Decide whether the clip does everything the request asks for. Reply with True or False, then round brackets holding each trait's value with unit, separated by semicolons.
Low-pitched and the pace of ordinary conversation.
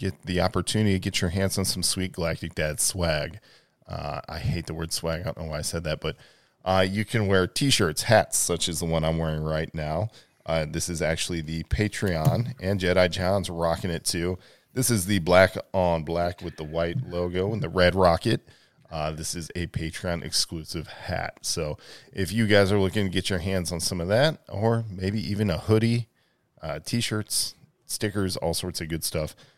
False (90 Hz; 210 wpm)